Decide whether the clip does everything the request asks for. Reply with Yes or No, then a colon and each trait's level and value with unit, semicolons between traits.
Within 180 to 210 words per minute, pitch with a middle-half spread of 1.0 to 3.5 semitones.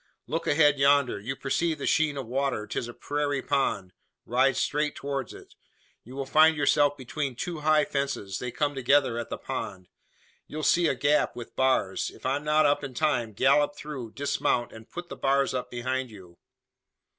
Yes: average, 185 wpm; average, 3.0 semitones